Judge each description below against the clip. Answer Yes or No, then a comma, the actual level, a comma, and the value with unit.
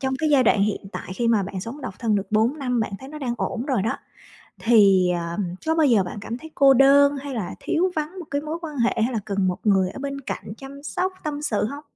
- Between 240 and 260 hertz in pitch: Yes, very high, 255 Hz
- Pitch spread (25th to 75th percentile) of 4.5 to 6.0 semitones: Yes, average, 5.2 semitones